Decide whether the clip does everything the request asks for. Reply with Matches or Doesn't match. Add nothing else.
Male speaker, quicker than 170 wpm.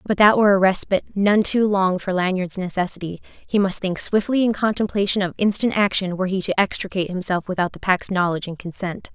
Doesn't match